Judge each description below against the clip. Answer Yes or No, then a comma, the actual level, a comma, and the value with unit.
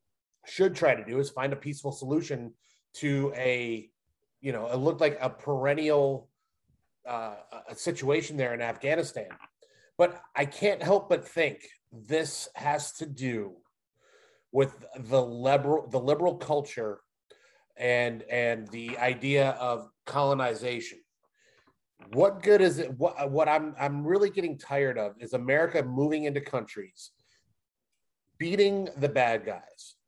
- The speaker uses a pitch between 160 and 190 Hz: No, medium, 140 Hz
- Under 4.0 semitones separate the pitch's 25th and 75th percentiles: Yes, average, 3.5 semitones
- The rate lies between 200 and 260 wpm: No, slow, 135 wpm